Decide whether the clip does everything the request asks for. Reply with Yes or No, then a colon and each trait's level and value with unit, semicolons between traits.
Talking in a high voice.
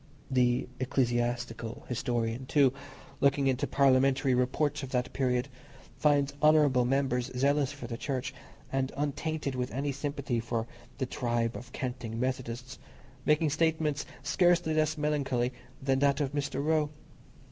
No: low, 135 Hz